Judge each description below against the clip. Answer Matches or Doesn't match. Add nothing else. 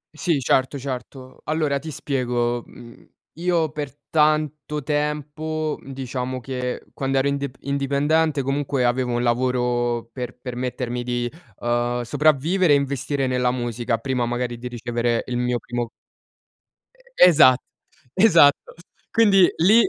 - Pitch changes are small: Doesn't match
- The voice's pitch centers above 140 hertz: Doesn't match